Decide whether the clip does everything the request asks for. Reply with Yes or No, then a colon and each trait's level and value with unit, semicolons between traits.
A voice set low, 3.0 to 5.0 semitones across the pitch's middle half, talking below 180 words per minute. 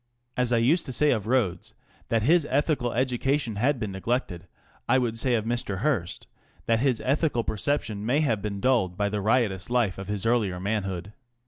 No: low, 115 Hz; average, 4.2 semitones; average, 190 wpm